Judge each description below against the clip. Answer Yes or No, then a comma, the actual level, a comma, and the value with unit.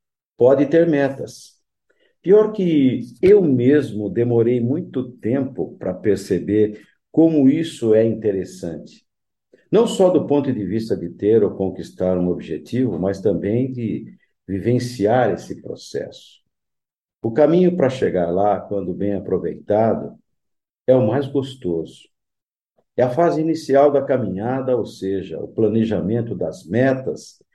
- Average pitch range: No, wide, 5.8 semitones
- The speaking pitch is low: Yes, low, 125 Hz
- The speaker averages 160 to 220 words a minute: No, average, 125 wpm